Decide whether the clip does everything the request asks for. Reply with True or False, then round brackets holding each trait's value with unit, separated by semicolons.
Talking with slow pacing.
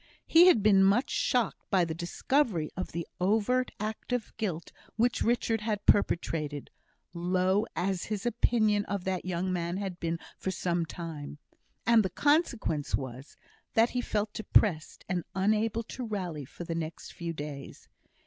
False (160 wpm)